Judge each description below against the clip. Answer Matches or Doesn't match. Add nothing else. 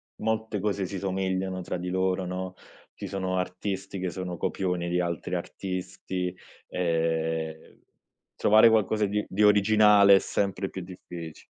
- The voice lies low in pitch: Matches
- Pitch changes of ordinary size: Doesn't match